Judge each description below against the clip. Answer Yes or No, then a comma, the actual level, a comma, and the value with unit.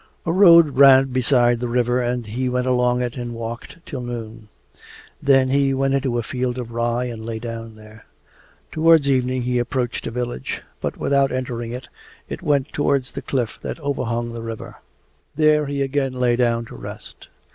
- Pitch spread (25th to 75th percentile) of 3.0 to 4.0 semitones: No, narrow, 2.4 semitones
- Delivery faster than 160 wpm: Yes, average, 180 wpm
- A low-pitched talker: Yes, low, 125 Hz